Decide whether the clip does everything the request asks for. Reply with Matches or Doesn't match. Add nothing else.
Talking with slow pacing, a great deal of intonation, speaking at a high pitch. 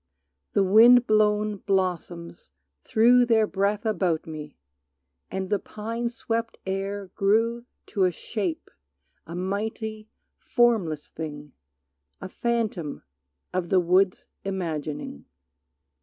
Doesn't match